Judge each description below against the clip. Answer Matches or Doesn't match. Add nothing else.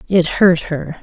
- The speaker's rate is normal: Matches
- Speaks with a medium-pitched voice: Matches